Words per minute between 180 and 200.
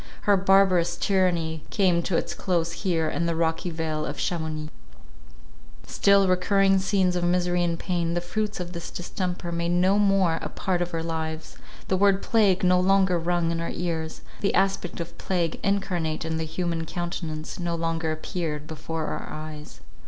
No: average, 165 wpm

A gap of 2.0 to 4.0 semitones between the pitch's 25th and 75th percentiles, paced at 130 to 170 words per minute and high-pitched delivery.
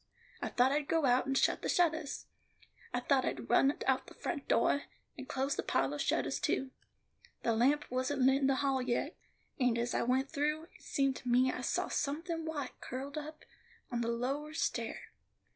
No: average, 2.9 semitones; average, 195 wpm; very high, 270 Hz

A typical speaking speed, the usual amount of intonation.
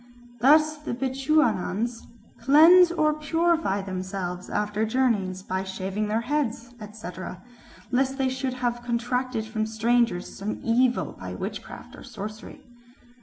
No: slow, 120 wpm; average, 4.3 semitones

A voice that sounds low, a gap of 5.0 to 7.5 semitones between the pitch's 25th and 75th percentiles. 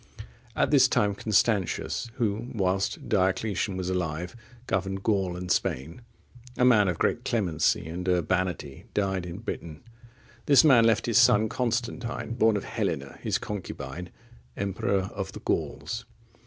No: very low, 95 Hz; average, 3.9 semitones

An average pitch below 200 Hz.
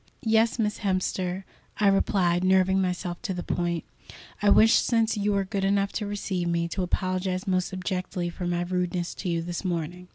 Yes: medium, 185 Hz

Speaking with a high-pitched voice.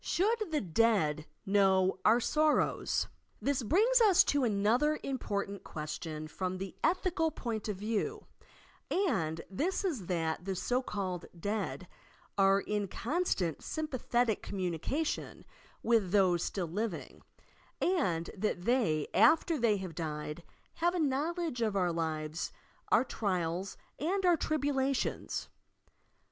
Yes: high, 210 Hz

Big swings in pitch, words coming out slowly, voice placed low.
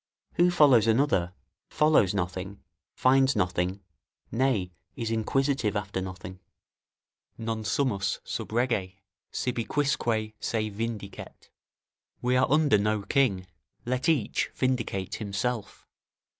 No: average, 4.8 semitones; slow, 105 wpm; low, 110 Hz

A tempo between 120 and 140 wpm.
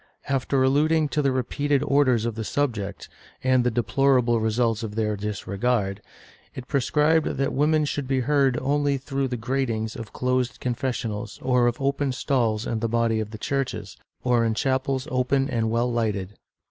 No: average, 170 wpm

